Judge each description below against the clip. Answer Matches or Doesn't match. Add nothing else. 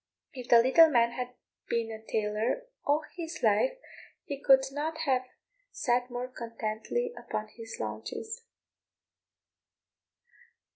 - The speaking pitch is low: Doesn't match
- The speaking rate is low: Matches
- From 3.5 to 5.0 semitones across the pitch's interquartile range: Matches